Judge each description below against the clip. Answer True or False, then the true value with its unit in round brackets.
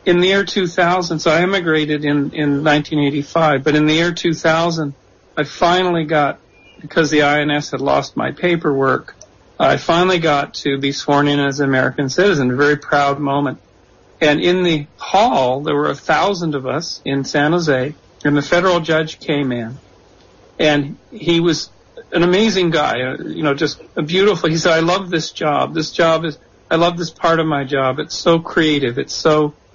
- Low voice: False (150 Hz)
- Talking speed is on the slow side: False (185 wpm)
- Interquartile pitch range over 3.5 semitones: False (3.0 semitones)